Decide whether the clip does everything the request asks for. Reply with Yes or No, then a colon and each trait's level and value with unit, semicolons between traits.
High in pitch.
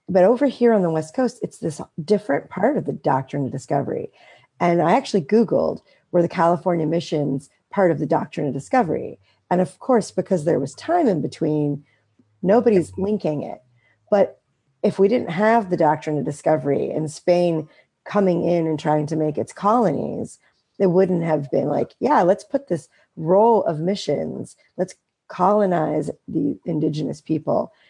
No: medium, 170 Hz